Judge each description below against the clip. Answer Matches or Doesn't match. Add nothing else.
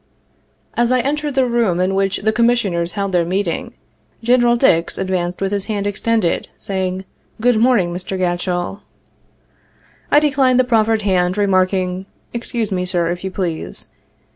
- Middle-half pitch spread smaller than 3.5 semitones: Doesn't match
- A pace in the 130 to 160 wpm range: Matches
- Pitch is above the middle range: Matches